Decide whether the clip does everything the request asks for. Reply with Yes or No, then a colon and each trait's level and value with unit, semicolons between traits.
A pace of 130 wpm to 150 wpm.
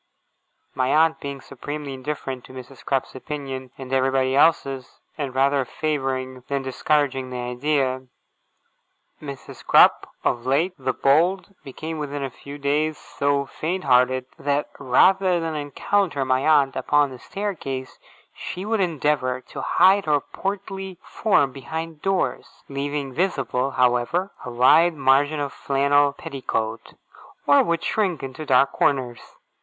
Yes: slow, 135 wpm